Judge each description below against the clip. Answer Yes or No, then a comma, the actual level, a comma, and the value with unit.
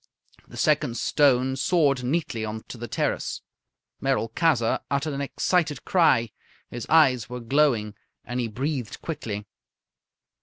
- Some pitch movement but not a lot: Yes, average, 4.2 semitones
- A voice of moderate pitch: No, low, 130 Hz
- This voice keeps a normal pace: No, slow, 125 wpm